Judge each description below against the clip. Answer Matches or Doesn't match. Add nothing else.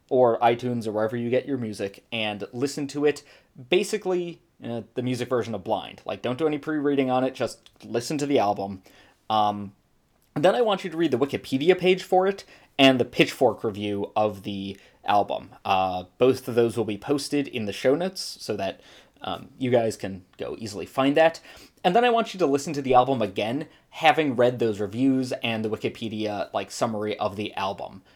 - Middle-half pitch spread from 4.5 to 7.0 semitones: Matches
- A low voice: Matches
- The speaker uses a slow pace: Doesn't match